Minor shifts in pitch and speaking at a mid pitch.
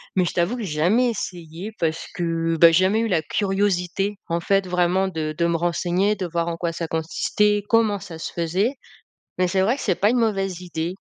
No: average, 3.2 semitones; medium, 180 Hz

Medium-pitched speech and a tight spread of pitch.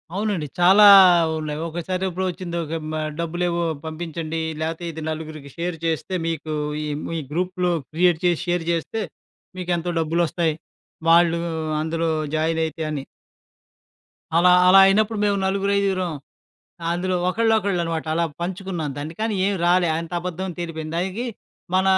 Yes: medium, 175 Hz; narrow, 2.3 semitones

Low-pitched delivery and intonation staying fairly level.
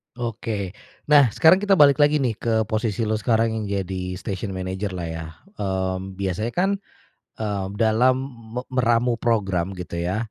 No: low, 105 Hz; average, 4.1 semitones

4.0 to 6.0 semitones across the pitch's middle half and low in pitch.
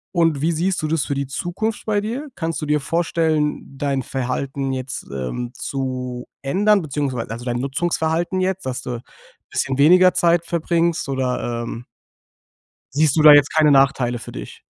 No: average, 4.6 semitones; medium, 145 Hz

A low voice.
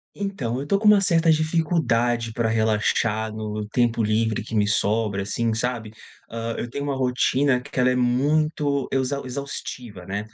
Yes: low, 120 Hz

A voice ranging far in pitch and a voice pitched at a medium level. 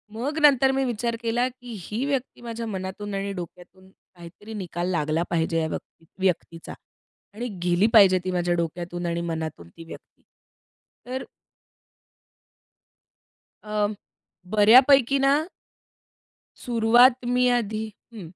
No: wide, 5.7 semitones; high, 205 Hz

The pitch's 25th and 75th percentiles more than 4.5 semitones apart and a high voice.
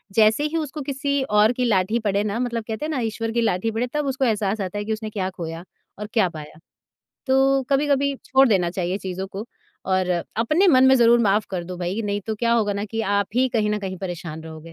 Yes: average, 4.9 semitones; high, 215 Hz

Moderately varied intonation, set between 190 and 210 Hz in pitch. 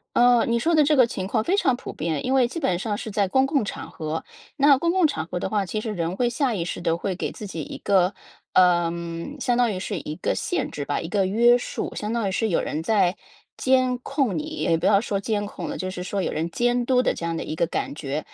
No: wide, 5.9 semitones; high, 205 Hz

